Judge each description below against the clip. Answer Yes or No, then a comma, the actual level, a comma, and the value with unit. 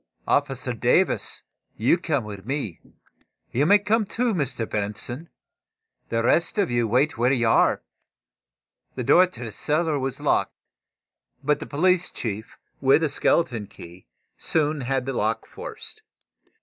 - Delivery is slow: No, average, 145 wpm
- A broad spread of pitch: Yes, wide, 6.4 semitones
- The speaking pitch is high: No, low, 135 Hz